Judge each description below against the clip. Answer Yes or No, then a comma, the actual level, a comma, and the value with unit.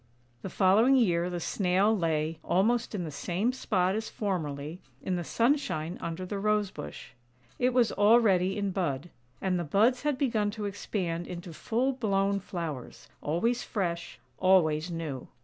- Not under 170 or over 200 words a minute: No, average, 155 wpm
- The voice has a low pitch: No, high, 190 Hz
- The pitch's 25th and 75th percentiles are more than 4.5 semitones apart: No, average, 4.2 semitones